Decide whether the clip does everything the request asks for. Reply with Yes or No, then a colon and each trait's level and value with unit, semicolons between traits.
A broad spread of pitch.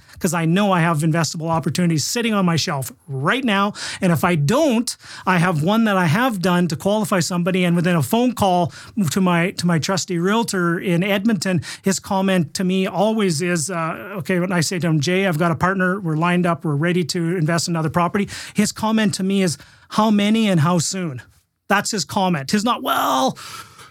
No: average, 2.7 semitones